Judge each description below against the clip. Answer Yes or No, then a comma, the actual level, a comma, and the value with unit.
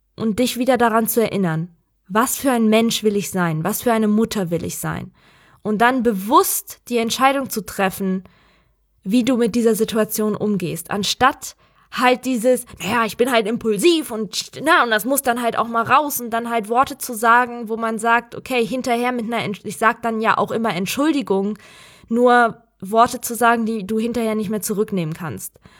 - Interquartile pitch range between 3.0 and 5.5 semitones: No, narrow, 2.5 semitones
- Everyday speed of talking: No, fast, 195 wpm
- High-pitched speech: Yes, high, 230 Hz